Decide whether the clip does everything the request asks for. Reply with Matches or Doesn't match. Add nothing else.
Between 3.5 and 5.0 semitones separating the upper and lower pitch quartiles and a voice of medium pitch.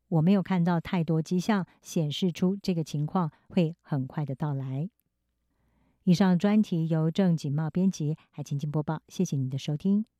Matches